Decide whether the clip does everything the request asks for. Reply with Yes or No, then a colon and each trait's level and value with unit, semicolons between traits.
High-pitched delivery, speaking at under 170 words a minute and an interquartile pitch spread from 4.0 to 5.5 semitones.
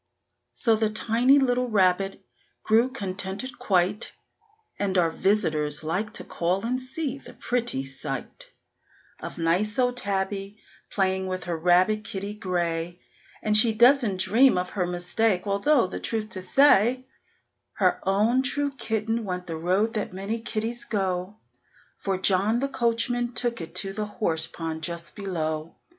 Yes: high, 200 Hz; average, 150 wpm; average, 4.3 semitones